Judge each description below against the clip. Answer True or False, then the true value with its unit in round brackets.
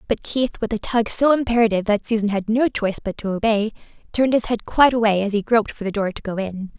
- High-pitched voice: True (220 Hz)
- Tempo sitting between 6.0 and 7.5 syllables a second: True (6.5 syllables/s)